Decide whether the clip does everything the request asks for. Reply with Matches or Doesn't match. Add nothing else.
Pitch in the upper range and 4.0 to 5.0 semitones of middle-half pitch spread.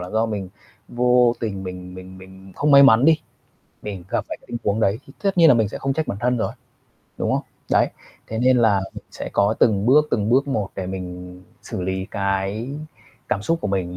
Doesn't match